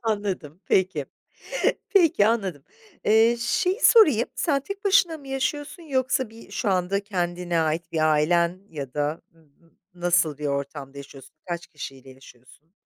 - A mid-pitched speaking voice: Yes, medium, 180 Hz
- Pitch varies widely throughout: Yes, wide, 8.7 semitones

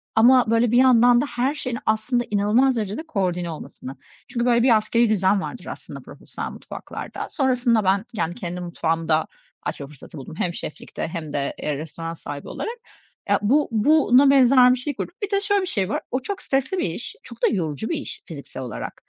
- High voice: Yes, high, 225 Hz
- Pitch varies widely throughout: Yes, wide, 7.0 semitones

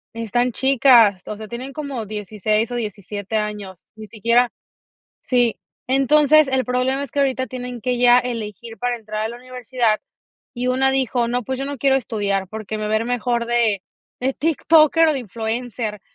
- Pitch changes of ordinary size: Yes, average, 3.1 semitones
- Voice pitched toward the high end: Yes, high, 240 Hz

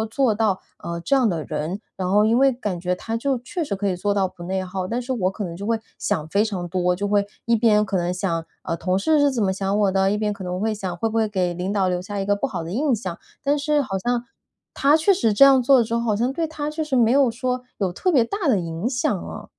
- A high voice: Yes, high, 210 Hz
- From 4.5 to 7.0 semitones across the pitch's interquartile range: Yes, average, 5.1 semitones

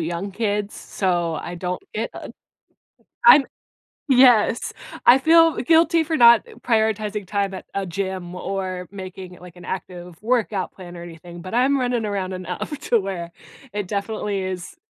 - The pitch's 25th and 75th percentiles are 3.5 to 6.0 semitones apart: Yes, average, 4.2 semitones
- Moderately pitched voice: No, high, 195 Hz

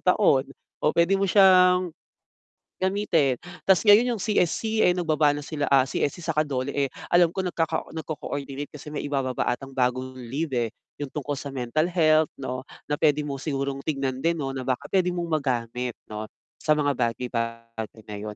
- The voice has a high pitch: No, medium, 145 Hz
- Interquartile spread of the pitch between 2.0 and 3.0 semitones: No, average, 4.6 semitones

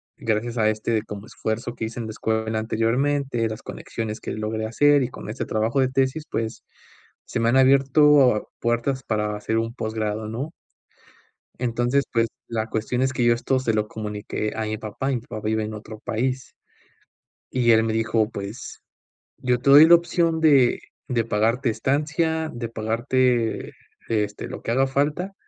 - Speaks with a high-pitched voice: No, low, 115 Hz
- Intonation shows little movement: No, average, 3.2 semitones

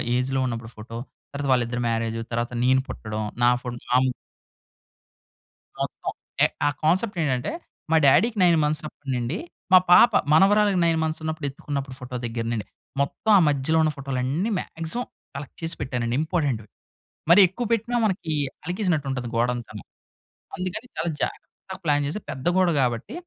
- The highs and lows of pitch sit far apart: Yes, wide, 5.9 semitones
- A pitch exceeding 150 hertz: No, medium, 140 Hz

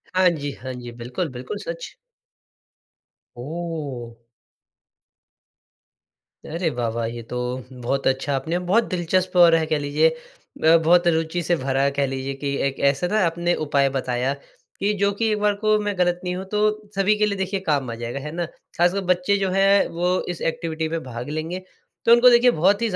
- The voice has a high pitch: No, medium, 165 Hz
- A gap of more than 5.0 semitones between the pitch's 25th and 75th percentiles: Yes, wide, 5.6 semitones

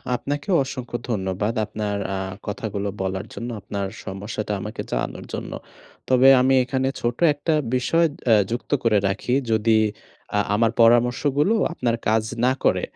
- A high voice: No, low, 115 Hz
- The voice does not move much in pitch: No, average, 3.6 semitones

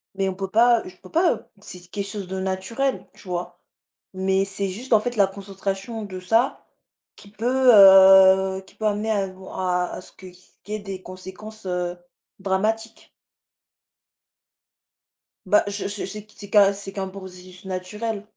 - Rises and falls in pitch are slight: Yes, narrow, 2.0 semitones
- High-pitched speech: Yes, high, 195 Hz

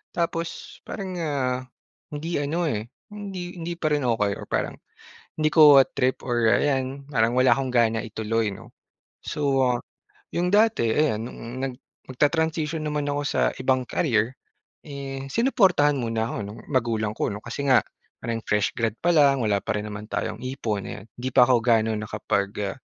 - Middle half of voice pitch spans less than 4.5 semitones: No, average, 5.0 semitones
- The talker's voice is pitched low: Yes, low, 130 Hz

